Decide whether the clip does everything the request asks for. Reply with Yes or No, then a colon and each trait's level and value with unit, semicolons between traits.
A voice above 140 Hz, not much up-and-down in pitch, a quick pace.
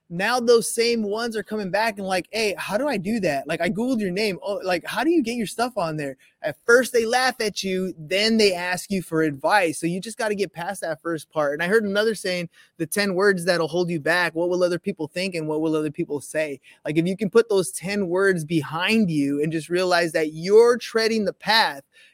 No: medium, 185 Hz; average, 4.7 semitones; fast, 250 wpm